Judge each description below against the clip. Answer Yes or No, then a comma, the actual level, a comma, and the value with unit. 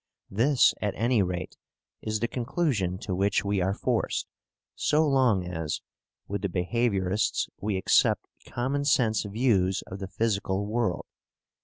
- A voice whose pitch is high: No, low, 105 Hz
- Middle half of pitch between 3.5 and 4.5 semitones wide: Yes, average, 4.1 semitones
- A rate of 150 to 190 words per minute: No, average, 140 wpm